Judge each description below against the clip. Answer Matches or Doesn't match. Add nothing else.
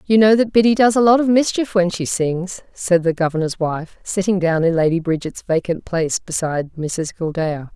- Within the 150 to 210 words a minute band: Matches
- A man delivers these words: Doesn't match